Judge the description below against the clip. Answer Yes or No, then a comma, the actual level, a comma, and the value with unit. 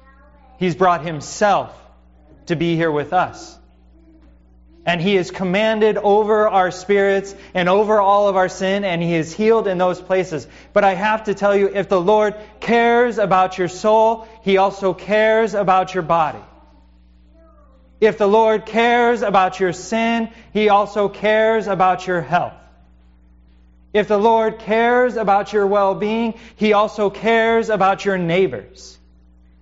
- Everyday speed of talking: Yes, average, 150 wpm